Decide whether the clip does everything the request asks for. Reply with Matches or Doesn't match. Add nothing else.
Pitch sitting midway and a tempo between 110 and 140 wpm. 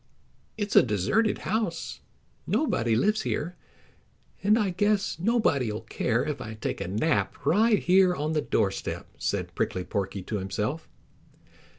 Matches